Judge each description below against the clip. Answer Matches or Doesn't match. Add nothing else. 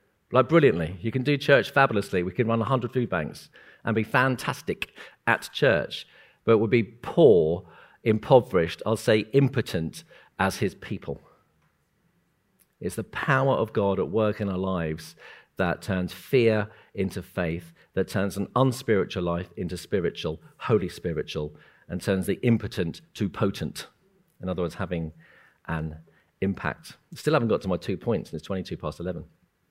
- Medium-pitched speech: Doesn't match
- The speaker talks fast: Doesn't match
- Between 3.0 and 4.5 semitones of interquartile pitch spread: Doesn't match